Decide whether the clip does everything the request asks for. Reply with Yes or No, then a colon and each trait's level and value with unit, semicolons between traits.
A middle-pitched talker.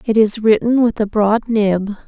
No: high, 215 Hz